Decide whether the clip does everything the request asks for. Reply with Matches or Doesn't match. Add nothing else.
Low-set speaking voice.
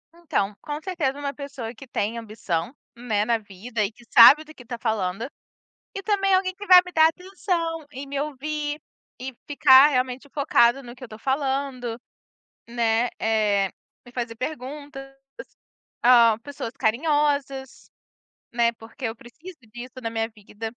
Doesn't match